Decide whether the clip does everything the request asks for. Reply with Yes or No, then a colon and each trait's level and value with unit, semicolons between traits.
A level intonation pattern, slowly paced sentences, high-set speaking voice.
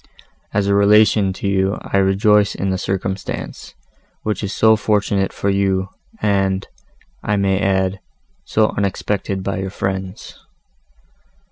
No: narrow, 1.3 semitones; slow, 130 wpm; low, 100 Hz